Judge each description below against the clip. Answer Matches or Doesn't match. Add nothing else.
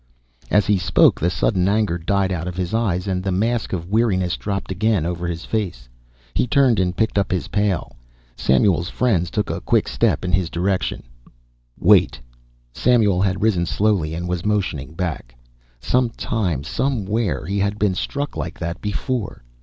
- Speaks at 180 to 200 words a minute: Doesn't match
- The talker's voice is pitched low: Matches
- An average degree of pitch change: Matches